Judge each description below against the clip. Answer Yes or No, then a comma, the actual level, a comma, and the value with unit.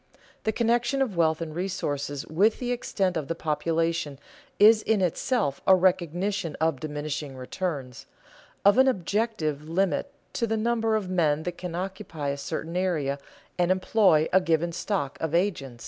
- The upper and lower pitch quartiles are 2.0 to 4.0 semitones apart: No, average, 4.9 semitones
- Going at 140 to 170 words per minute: Yes, average, 160 wpm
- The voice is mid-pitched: Yes, medium, 175 Hz